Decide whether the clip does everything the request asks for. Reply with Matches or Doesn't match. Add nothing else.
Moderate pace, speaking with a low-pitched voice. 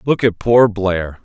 Matches